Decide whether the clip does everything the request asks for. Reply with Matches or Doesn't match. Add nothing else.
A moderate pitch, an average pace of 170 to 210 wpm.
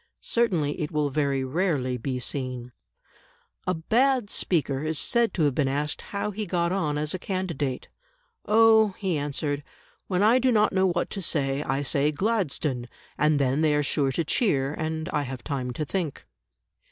Matches